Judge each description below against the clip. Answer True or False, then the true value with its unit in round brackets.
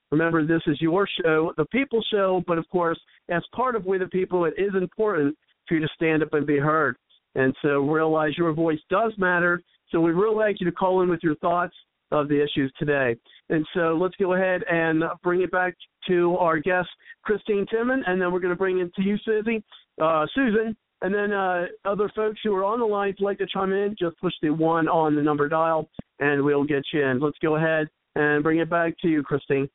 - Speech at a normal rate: False (230 wpm)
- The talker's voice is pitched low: False (175 Hz)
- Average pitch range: True (3.6 semitones)